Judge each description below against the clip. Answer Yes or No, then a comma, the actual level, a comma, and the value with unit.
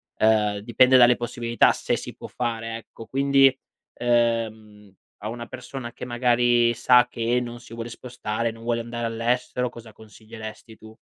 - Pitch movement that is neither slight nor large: No, narrow, 1.3 semitones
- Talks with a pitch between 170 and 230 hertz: No, low, 120 Hz